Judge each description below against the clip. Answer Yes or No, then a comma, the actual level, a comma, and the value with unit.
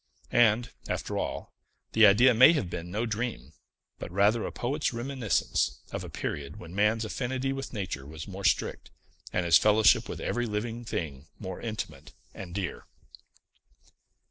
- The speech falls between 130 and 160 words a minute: Yes, average, 155 wpm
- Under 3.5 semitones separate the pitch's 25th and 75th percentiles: No, average, 5.1 semitones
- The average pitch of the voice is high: No, low, 105 Hz